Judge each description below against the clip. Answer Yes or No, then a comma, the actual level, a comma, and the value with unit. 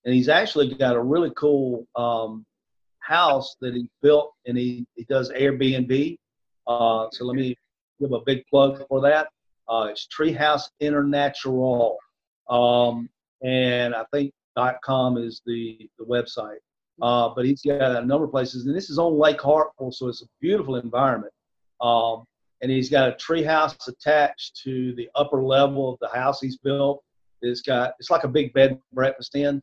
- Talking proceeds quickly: No, average, 170 wpm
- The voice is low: Yes, low, 130 Hz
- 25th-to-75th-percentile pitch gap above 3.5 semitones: No, average, 2.8 semitones